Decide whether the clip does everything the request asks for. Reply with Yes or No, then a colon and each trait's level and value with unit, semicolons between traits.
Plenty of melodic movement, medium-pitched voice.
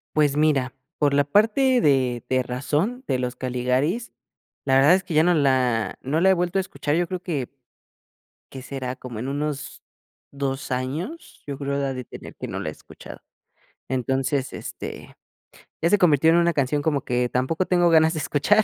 No: average, 4.6 semitones; medium, 145 Hz